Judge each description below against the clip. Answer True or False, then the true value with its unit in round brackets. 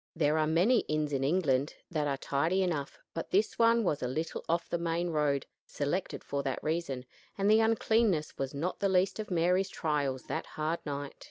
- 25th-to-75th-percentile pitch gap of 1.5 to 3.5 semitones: False (4.5 semitones)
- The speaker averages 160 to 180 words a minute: False (195 wpm)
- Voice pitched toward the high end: False (160 Hz)